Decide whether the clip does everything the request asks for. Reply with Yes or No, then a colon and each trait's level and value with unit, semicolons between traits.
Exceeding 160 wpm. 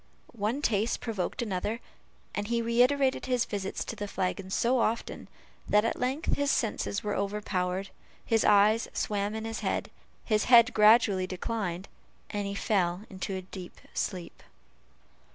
No: average, 150 wpm